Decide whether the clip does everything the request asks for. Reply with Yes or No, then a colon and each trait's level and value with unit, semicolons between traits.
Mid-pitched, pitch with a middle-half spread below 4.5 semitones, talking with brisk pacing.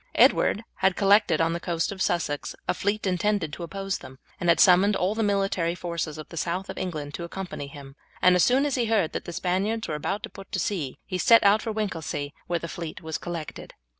Yes: medium, 180 Hz; average, 3.5 semitones; fast, 230 wpm